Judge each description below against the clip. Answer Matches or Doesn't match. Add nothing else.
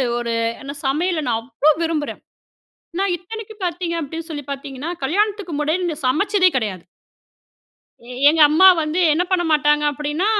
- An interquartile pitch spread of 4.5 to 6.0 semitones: Doesn't match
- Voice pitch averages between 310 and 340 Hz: Matches